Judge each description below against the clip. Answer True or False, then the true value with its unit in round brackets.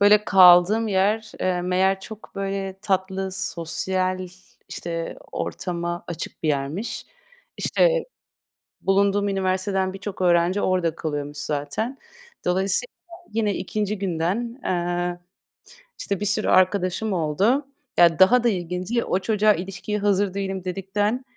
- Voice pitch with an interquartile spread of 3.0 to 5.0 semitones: False (2.5 semitones)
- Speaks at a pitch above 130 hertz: True (190 Hz)